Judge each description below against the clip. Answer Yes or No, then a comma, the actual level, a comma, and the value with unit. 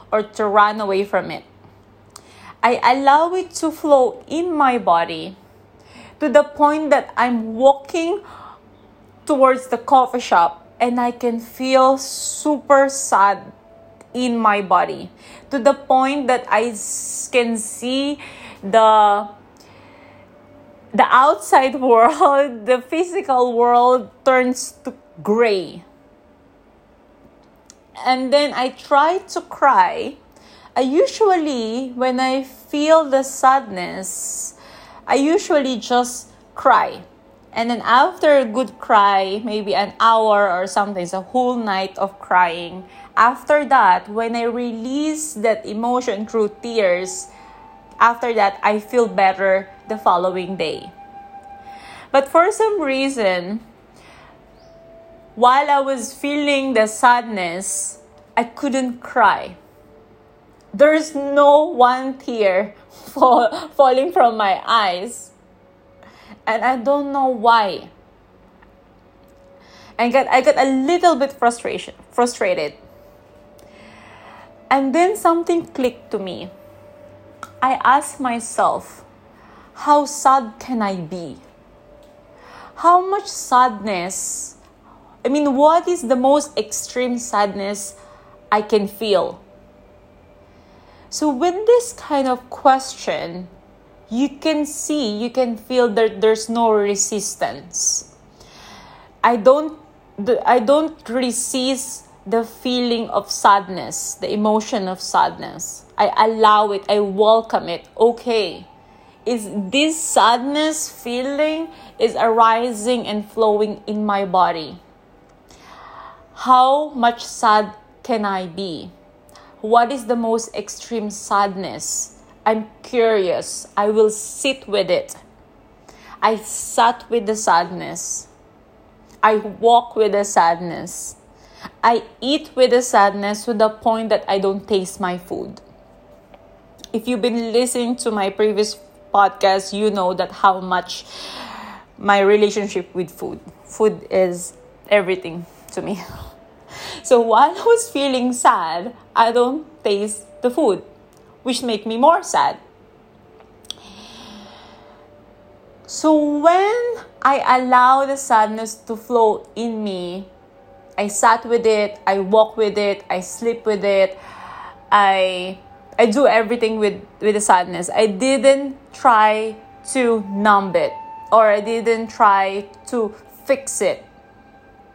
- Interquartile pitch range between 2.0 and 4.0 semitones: No, average, 4.9 semitones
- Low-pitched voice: No, high, 230 Hz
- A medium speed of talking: No, slow, 115 wpm